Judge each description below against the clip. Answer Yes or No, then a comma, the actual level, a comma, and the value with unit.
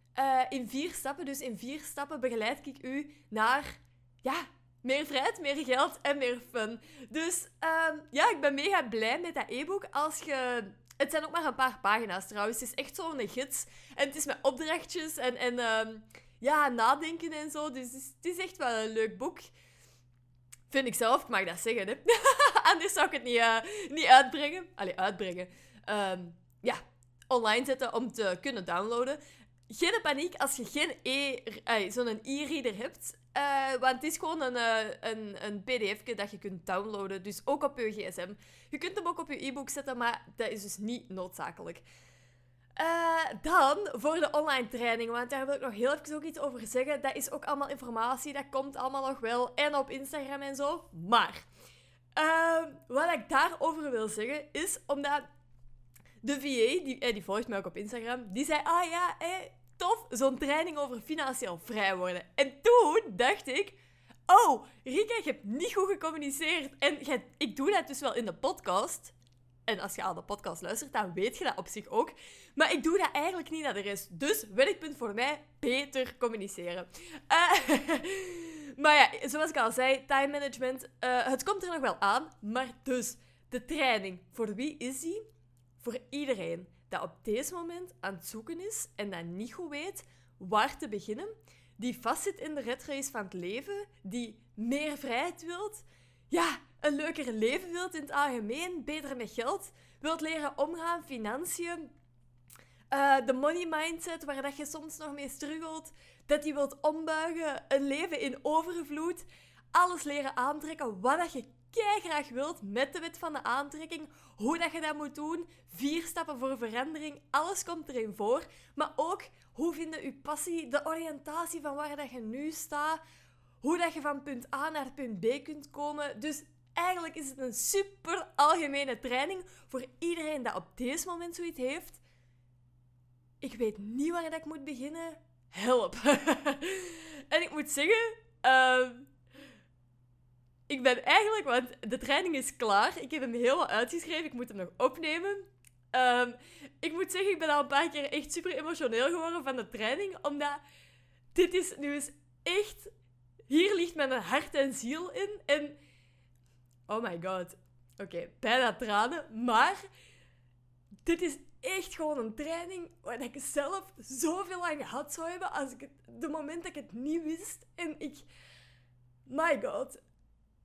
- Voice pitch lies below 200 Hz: No, very high, 275 Hz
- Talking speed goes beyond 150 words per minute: Yes, average, 180 wpm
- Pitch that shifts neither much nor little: No, wide, 6.0 semitones